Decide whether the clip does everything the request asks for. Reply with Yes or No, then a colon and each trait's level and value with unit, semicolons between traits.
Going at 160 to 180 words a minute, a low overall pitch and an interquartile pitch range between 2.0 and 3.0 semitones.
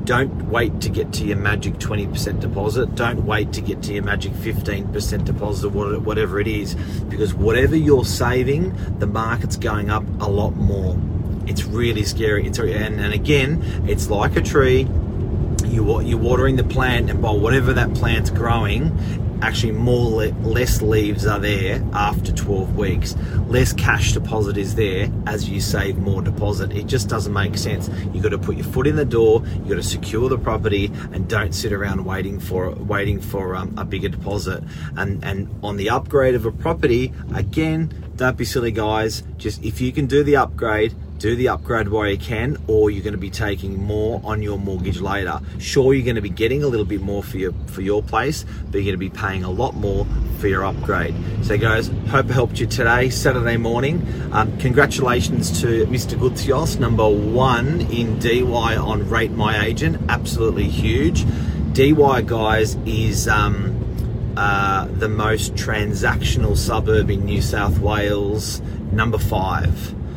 Yes: average, 175 wpm; low, 105 Hz; narrow, 2.4 semitones